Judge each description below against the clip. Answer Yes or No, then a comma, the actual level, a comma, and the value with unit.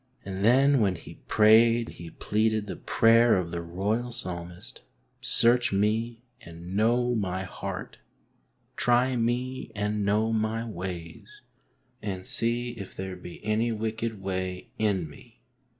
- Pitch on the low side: Yes, low, 110 Hz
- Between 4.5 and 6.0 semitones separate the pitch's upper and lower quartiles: No, average, 3.7 semitones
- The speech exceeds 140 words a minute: No, slow, 135 wpm